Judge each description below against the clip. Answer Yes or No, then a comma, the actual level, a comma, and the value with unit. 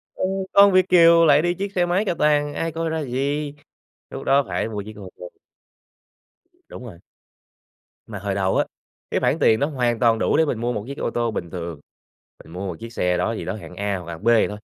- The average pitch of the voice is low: Yes, low, 120 Hz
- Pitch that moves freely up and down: Yes, wide, 7.7 semitones